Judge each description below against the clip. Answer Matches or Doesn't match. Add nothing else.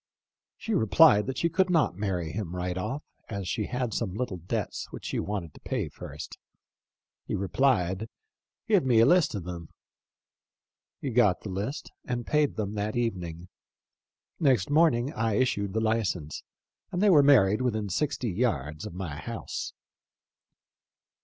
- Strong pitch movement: Matches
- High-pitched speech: Doesn't match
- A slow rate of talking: Doesn't match